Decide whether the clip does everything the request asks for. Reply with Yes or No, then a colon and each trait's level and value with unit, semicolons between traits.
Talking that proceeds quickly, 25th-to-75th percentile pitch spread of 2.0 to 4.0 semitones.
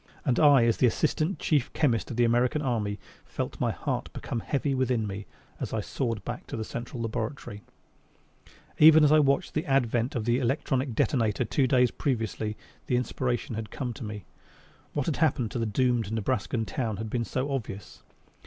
No: average, 180 wpm; average, 3.3 semitones